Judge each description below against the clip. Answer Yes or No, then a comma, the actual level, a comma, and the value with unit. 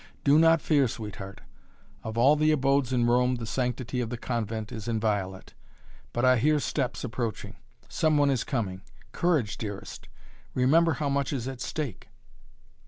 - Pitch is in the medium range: No, low, 125 Hz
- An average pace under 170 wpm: Yes, average, 160 wpm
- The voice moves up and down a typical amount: Yes, average, 3.9 semitones